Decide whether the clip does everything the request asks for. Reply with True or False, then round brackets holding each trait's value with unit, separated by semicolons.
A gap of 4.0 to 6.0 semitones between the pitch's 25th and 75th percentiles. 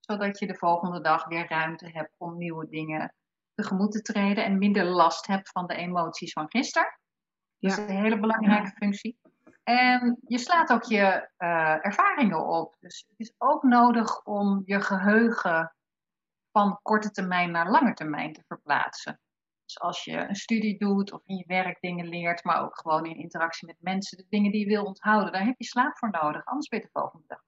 True (4.3 semitones)